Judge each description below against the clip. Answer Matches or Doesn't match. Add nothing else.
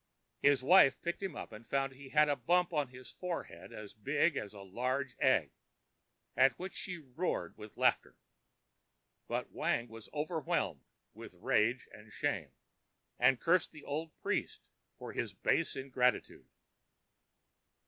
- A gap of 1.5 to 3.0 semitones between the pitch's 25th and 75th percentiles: Doesn't match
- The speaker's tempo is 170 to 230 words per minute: Doesn't match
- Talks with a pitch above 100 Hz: Matches